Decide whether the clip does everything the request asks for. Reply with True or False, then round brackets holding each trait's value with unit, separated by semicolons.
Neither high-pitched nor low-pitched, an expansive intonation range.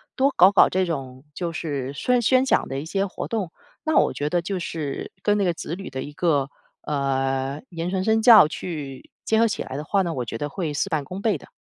True (170 Hz; 5.8 semitones)